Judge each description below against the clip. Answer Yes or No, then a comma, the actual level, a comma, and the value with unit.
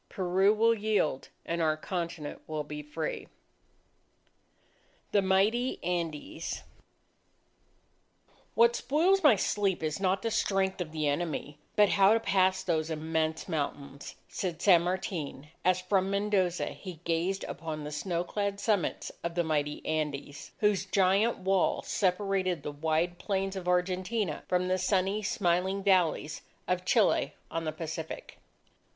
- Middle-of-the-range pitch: Yes, medium, 180 Hz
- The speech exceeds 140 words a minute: No, slow, 135 wpm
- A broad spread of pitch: No, average, 3.6 semitones